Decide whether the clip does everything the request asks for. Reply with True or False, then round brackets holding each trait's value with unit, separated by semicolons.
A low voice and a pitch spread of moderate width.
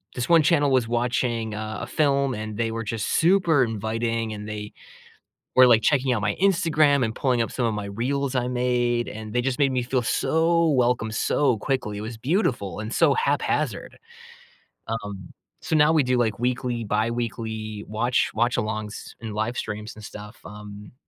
True (120 Hz; 3.5 semitones)